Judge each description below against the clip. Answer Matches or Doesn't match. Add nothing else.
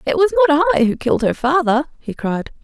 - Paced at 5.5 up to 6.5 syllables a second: Matches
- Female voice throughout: Matches